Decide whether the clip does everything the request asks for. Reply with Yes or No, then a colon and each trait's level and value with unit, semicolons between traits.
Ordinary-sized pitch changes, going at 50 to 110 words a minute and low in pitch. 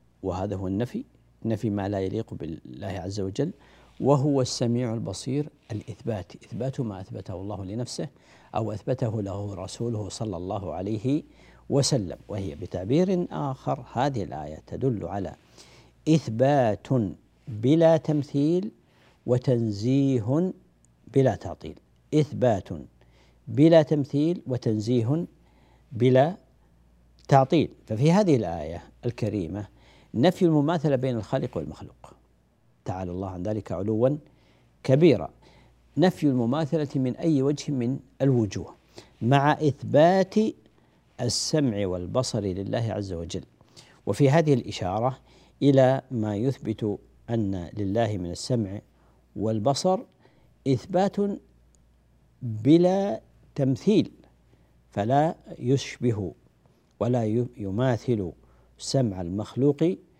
No: wide, 6.3 semitones; average, 95 wpm; low, 120 Hz